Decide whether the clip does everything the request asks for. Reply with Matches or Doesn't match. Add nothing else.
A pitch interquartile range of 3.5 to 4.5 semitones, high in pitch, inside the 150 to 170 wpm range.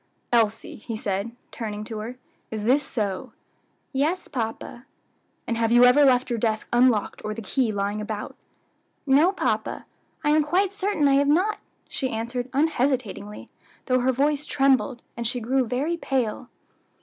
Matches